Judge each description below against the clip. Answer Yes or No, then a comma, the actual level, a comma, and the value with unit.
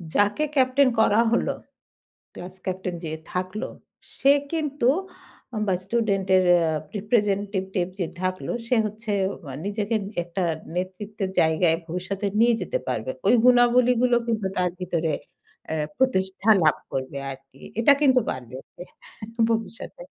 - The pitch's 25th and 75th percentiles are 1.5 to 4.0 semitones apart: No, average, 4.5 semitones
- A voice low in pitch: No, high, 200 Hz